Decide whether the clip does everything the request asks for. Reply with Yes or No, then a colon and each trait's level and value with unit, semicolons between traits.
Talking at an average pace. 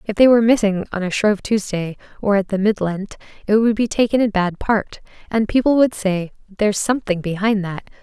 No: fast, 210 wpm